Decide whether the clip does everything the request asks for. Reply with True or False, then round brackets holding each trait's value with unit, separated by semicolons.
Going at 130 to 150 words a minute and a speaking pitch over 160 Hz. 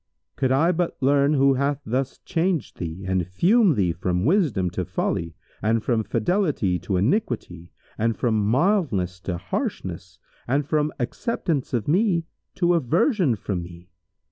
False (145 wpm; 125 Hz)